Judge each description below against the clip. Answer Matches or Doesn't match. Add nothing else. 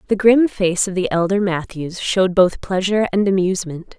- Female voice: Matches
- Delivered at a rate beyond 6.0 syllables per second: Doesn't match